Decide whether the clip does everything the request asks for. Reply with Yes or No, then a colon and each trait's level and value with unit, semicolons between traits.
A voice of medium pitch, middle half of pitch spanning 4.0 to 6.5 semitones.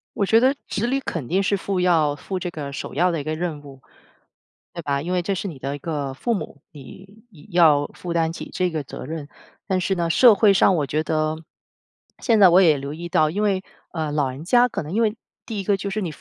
Yes: medium, 170 Hz; average, 4.5 semitones